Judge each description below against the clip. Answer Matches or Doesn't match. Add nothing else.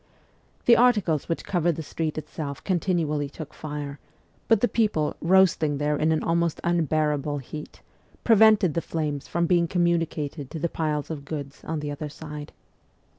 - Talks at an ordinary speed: Matches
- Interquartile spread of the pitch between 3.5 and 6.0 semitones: Doesn't match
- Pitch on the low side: Doesn't match